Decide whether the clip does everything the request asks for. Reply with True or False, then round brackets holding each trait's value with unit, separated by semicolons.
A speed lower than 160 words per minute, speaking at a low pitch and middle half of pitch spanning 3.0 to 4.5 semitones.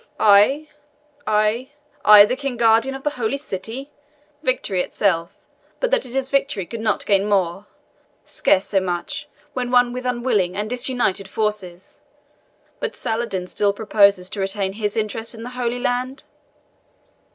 False (150 wpm; 220 Hz; 4.0 semitones)